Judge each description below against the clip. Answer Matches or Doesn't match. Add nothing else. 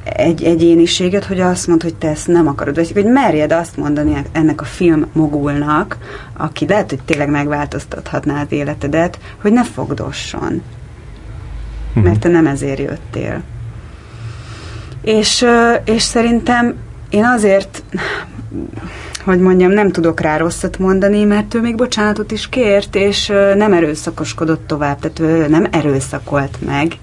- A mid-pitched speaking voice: Matches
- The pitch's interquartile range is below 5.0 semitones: Doesn't match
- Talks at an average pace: Matches